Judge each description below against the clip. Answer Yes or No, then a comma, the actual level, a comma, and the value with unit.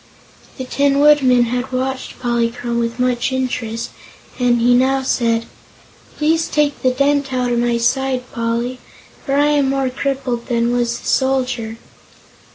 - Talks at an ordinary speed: Yes, average, 150 wpm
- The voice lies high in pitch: Yes, very high, 255 Hz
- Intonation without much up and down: Yes, narrow, 2.1 semitones